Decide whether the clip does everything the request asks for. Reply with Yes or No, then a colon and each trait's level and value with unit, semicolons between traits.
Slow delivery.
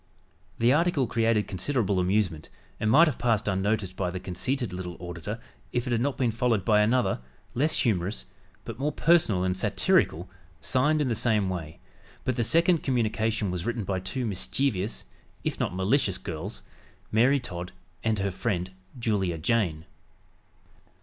No: average, 155 wpm